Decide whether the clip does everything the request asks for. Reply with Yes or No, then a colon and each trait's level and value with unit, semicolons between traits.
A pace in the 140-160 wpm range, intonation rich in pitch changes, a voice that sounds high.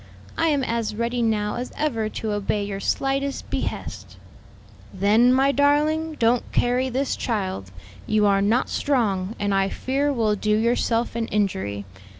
No: average, 155 wpm; average, 4.2 semitones; high, 230 Hz